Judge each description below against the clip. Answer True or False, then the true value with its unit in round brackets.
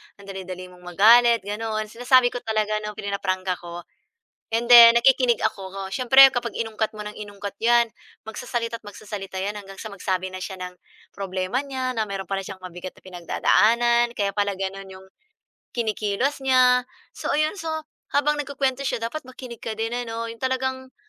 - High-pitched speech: True (220 Hz)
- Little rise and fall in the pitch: False (3.9 semitones)